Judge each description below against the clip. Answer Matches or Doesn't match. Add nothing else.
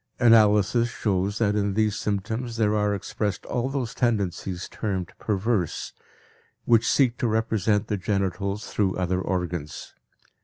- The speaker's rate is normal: Doesn't match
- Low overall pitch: Matches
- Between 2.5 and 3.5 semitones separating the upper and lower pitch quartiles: Matches